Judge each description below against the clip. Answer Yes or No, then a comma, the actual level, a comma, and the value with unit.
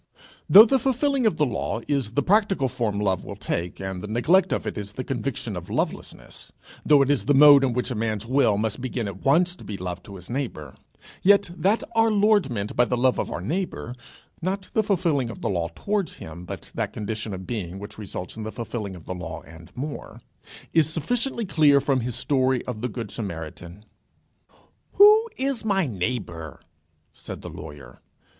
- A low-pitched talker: Yes, low, 125 Hz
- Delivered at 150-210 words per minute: Yes, average, 200 wpm